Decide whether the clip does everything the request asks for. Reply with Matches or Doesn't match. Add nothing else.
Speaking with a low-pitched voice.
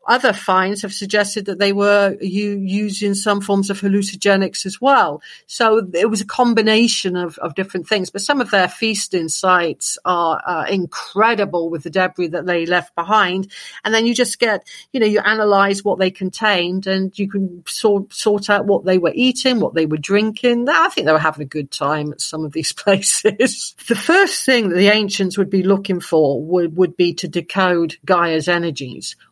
Doesn't match